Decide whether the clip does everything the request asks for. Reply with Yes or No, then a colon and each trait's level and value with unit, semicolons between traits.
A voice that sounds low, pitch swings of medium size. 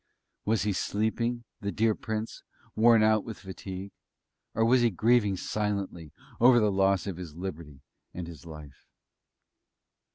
Yes: low, 100 Hz; average, 3.7 semitones